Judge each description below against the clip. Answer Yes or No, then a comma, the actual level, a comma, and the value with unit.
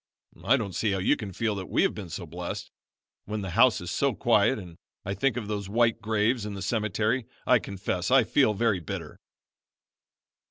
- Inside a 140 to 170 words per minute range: No, average, 200 wpm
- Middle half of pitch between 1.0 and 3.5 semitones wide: Yes, average, 3.2 semitones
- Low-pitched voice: Yes, low, 105 Hz